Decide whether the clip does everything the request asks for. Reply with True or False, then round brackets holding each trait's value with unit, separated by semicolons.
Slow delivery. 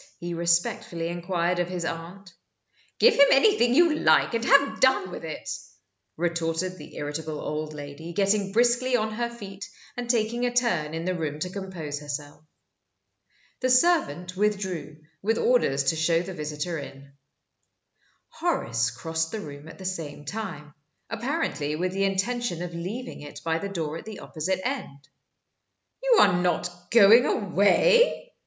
False (155 wpm)